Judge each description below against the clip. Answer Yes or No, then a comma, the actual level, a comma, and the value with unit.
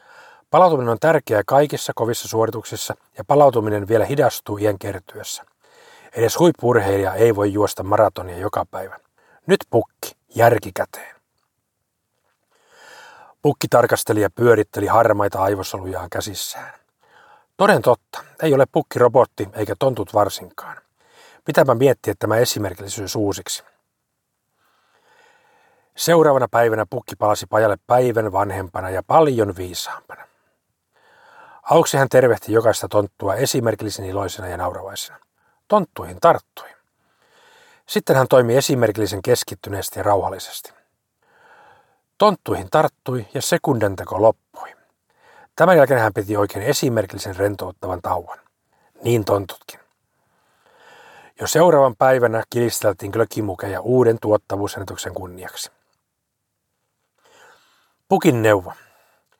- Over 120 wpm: No, average, 100 wpm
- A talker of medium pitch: No, low, 110 Hz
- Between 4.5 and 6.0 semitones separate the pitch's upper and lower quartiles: Yes, wide, 5.5 semitones